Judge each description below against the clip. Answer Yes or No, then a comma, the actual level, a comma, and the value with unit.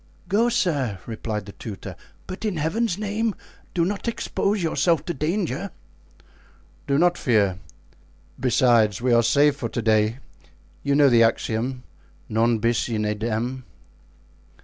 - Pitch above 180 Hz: No, low, 130 Hz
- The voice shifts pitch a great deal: Yes, wide, 7.5 semitones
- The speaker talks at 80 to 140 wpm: Yes, slow, 135 wpm